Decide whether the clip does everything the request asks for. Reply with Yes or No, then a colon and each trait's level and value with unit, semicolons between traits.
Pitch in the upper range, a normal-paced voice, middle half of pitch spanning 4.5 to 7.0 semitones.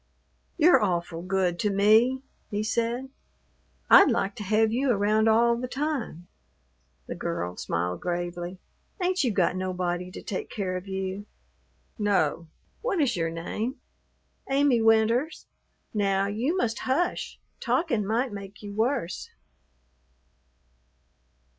No: high, 210 Hz; slow, 125 wpm; average, 4.9 semitones